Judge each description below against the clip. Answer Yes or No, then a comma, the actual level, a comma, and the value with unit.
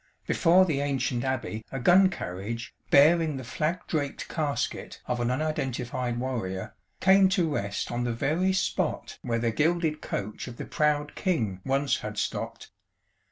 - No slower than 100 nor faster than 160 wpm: Yes, average, 155 wpm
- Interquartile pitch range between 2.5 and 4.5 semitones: No, average, 5.1 semitones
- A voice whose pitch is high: No, low, 135 Hz